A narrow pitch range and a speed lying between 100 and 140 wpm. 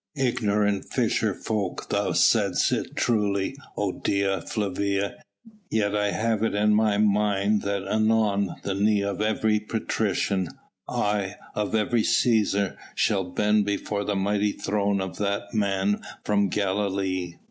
Yes: narrow, 1.2 semitones; slow, 135 wpm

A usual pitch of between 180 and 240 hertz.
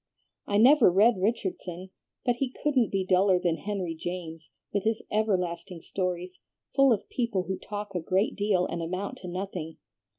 Yes: high, 190 Hz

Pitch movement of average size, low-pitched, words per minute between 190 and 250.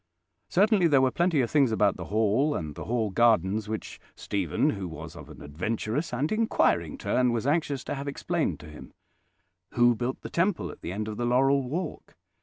No: wide, 5.7 semitones; low, 120 Hz; average, 200 wpm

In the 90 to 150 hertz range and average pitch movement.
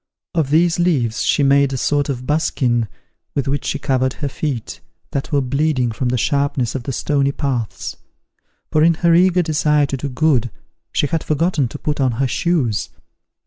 Yes: medium, 140 Hz; average, 3.3 semitones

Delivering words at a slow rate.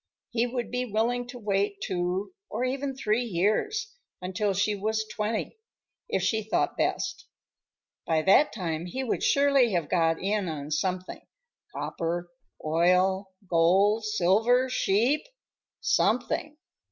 Yes: slow, 125 wpm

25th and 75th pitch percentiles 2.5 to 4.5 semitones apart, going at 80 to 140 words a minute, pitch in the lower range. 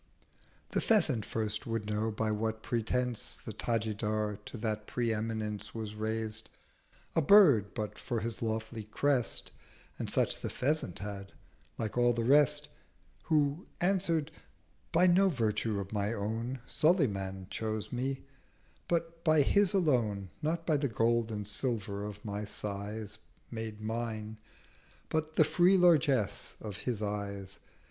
No: average, 4.9 semitones; slow, 135 wpm; low, 110 Hz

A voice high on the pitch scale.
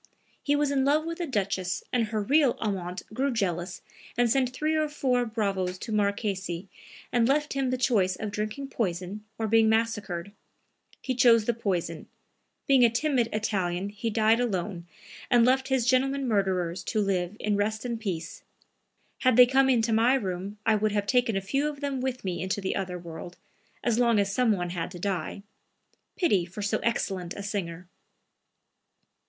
Yes: high, 215 Hz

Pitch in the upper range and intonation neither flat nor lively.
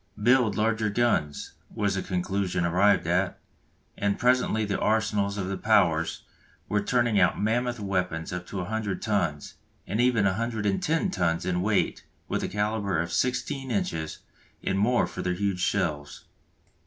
No: low, 100 Hz; average, 3.5 semitones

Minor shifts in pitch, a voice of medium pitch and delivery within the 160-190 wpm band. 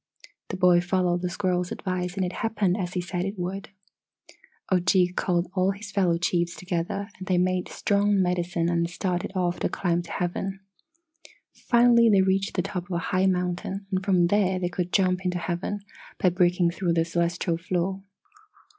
Yes: narrow, 1.6 semitones; medium, 180 Hz; average, 180 wpm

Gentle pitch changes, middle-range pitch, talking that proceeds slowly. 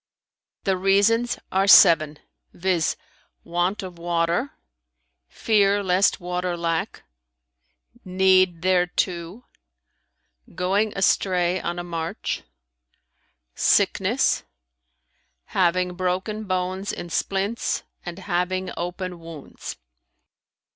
Yes: narrow, 1.9 semitones; medium, 180 Hz; slow, 85 wpm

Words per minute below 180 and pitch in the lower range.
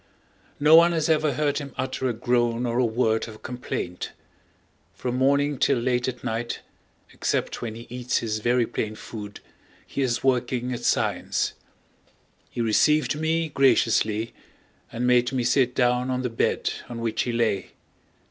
Yes: average, 160 wpm; low, 125 Hz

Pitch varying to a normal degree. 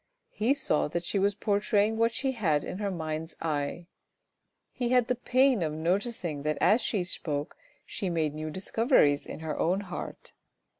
No: wide, 6.2 semitones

